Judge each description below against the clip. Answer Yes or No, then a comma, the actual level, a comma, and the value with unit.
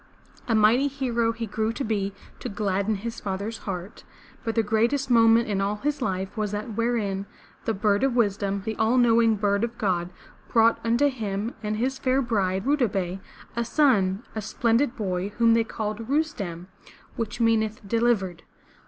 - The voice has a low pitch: No, high, 220 Hz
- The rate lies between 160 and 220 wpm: Yes, average, 180 wpm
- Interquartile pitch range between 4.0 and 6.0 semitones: No, average, 2.8 semitones